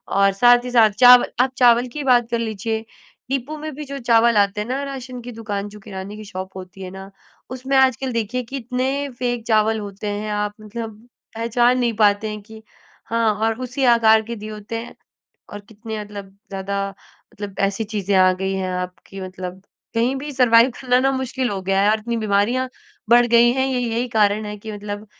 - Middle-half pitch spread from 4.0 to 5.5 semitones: No, average, 3.4 semitones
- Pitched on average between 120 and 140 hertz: No, high, 220 Hz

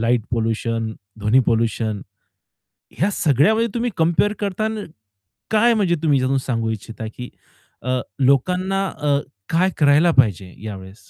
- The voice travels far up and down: Yes, wide, 8.5 semitones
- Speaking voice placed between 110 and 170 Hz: Yes, low, 135 Hz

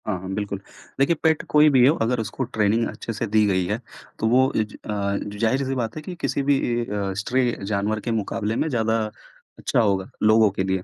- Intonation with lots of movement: No, average, 3.7 semitones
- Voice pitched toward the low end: Yes, low, 110 Hz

